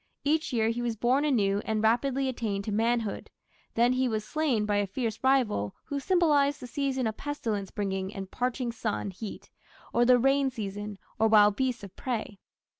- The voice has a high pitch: Yes, high, 230 Hz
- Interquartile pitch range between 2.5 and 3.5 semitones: No, average, 4.1 semitones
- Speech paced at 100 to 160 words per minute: No, average, 185 wpm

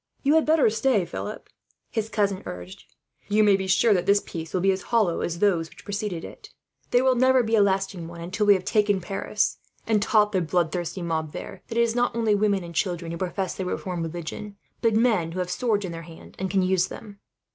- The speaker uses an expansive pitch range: No, average, 3.6 semitones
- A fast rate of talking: Yes, fast, 230 wpm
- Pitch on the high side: Yes, high, 195 Hz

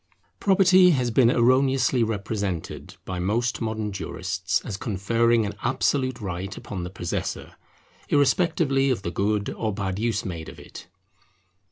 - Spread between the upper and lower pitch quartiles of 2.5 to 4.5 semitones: No, average, 5.0 semitones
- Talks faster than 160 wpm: No, average, 140 wpm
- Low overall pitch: Yes, low, 110 Hz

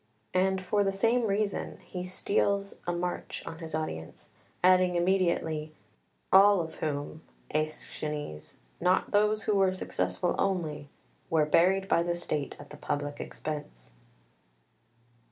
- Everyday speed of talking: No, slow, 130 wpm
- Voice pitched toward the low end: No, medium, 175 Hz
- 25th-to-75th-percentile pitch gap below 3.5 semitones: No, average, 3.9 semitones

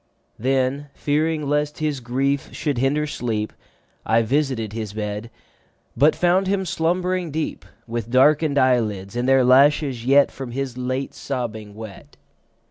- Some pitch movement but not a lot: Yes, average, 4.1 semitones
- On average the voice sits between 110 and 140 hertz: Yes, low, 135 Hz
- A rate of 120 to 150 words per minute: Yes, average, 140 wpm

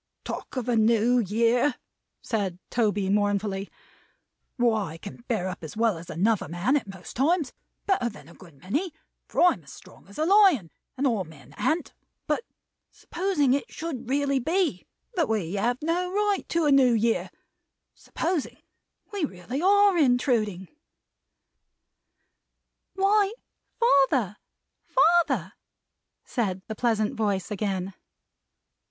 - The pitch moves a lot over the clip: Yes, wide, 7.5 semitones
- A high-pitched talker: Yes, high, 235 Hz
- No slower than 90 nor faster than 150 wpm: Yes, slow, 135 wpm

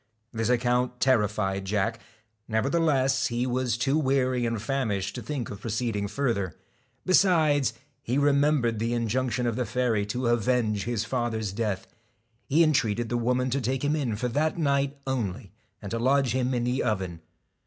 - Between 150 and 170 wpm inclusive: Yes, average, 165 wpm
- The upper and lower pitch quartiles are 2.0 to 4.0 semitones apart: Yes, average, 3.3 semitones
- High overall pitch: No, low, 120 Hz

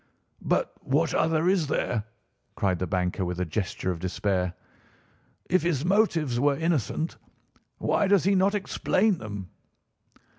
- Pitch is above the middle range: No, medium, 145 Hz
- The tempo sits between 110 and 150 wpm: Yes, average, 140 wpm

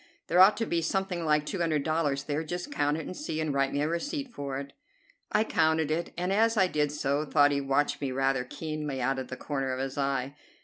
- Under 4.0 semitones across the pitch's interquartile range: Yes, average, 3.5 semitones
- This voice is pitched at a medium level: Yes, medium, 150 Hz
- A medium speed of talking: No, fast, 245 wpm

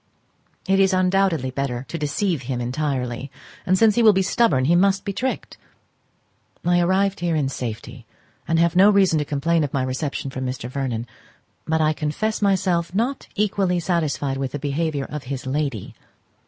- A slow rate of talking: No, average, 175 wpm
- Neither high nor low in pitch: Yes, medium, 155 Hz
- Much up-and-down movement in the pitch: Yes, wide, 5.9 semitones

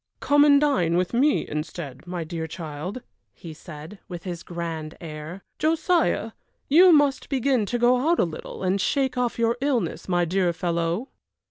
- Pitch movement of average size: No, wide, 7.9 semitones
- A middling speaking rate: Yes, average, 165 wpm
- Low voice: No, medium, 185 Hz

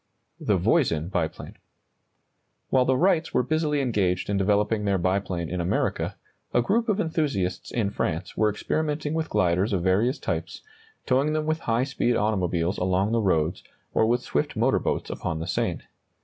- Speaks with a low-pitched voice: Yes, low, 105 Hz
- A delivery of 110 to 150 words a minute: No, average, 165 wpm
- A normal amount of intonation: No, wide, 7.1 semitones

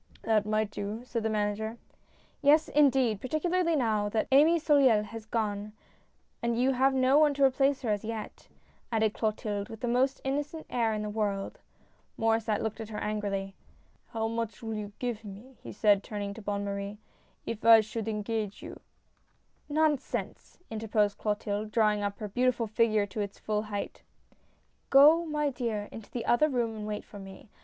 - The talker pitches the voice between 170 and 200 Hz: No, high, 220 Hz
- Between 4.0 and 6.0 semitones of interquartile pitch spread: No, average, 3.4 semitones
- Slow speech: No, average, 190 wpm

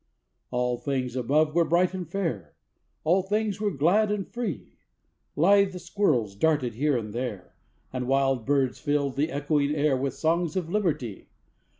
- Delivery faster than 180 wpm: No, average, 155 wpm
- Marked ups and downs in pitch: Yes, wide, 5.8 semitones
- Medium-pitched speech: Yes, medium, 150 Hz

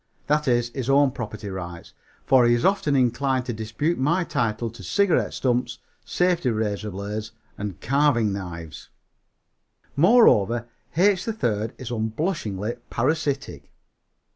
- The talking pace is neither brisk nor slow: No, slow, 125 wpm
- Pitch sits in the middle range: No, low, 120 Hz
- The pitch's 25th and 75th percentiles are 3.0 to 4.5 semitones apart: No, average, 5.2 semitones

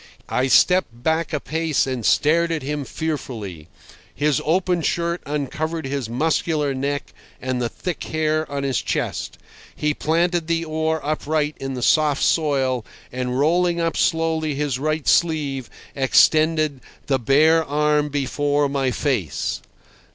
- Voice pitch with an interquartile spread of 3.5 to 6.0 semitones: No, average, 3.0 semitones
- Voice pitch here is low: No, medium, 150 Hz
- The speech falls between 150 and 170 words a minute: No, average, 140 wpm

